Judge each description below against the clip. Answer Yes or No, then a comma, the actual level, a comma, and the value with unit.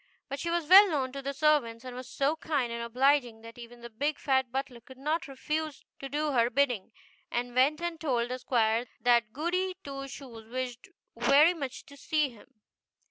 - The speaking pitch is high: Yes, very high, 270 Hz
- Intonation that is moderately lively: Yes, average, 3.8 semitones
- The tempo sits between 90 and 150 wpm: No, average, 195 wpm